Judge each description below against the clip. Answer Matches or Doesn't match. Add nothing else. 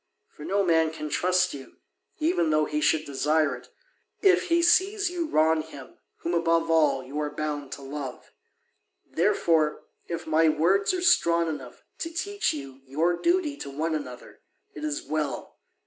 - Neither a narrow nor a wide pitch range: Matches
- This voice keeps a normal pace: Matches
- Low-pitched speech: Doesn't match